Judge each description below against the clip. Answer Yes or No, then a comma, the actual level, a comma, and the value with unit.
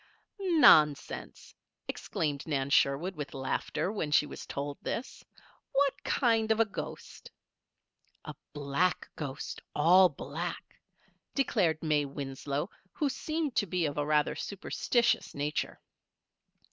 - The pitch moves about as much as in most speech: No, wide, 7.3 semitones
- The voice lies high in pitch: No, medium, 155 Hz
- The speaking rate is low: Yes, slow, 120 wpm